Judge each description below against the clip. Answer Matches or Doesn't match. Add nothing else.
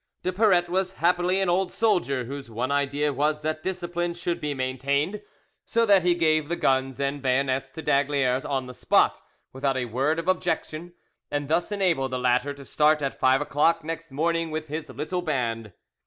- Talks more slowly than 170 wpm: Doesn't match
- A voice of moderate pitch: Matches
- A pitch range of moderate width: Matches